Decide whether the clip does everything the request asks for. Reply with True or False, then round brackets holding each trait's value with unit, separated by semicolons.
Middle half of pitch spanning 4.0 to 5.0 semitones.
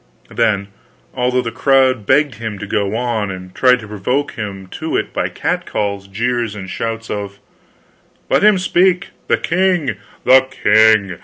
True (4.6 semitones)